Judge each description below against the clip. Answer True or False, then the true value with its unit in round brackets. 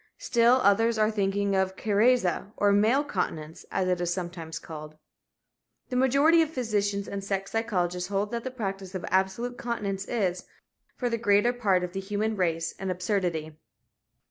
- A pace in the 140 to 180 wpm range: True (165 wpm)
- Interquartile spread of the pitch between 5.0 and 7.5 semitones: False (4.1 semitones)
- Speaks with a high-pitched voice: True (200 Hz)